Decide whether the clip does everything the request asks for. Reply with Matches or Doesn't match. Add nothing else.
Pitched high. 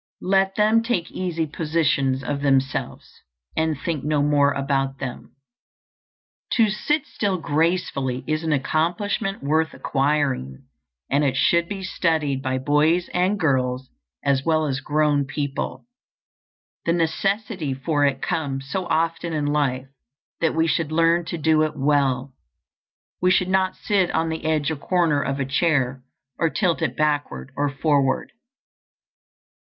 Doesn't match